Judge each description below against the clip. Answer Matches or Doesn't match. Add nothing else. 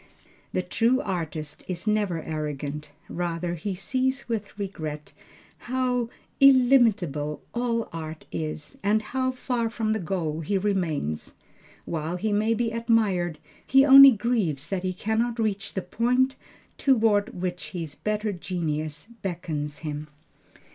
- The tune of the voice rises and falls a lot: Matches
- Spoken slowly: Matches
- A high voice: Matches